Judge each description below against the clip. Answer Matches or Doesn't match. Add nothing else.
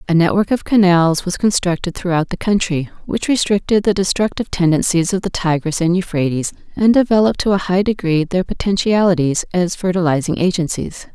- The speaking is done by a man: Doesn't match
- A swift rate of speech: Doesn't match